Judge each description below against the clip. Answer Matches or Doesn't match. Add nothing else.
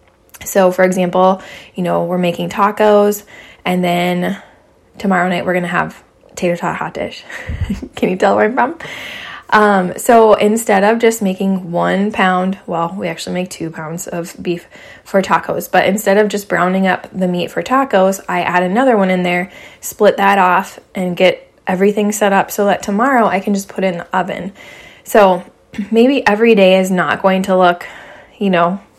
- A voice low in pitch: Doesn't match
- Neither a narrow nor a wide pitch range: Doesn't match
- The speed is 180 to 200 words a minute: Matches